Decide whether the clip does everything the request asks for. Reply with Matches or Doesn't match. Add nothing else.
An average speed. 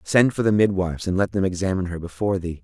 Doesn't match